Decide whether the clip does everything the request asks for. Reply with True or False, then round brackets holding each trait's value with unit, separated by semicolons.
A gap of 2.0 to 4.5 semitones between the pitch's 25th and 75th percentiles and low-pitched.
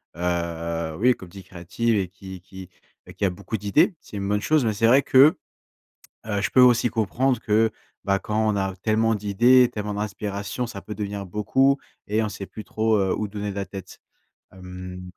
True (2.8 semitones; 105 Hz)